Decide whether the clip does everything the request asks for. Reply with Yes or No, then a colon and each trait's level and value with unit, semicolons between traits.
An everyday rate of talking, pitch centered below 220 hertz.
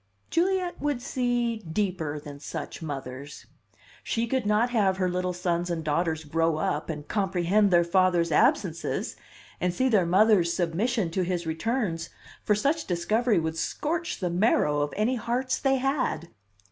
Yes: average, 155 wpm; medium, 185 Hz